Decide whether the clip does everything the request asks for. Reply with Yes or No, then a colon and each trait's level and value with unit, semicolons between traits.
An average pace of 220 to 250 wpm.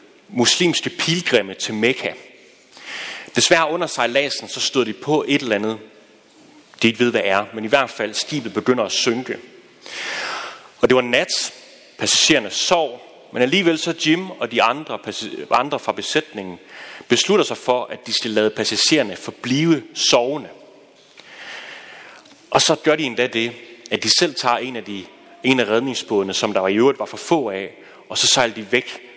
No: average, 170 wpm